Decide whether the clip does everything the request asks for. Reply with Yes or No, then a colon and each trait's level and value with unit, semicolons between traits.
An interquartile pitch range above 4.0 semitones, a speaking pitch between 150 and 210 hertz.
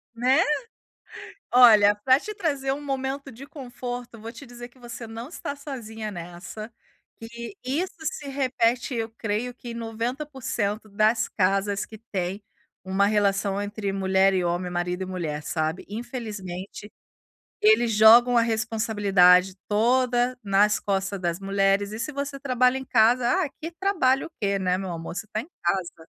No: average, 4.4 semitones; high, 225 Hz